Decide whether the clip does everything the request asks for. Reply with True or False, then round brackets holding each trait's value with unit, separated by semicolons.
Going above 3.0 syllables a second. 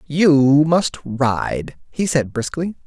False (2.8 syllables/s)